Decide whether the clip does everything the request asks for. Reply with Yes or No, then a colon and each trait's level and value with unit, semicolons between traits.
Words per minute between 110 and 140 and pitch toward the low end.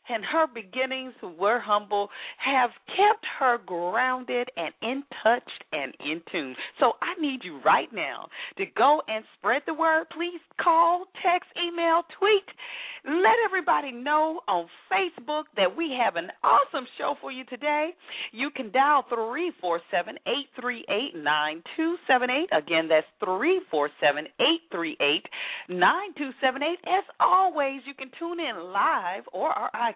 No: slow, 135 wpm; very high, 285 Hz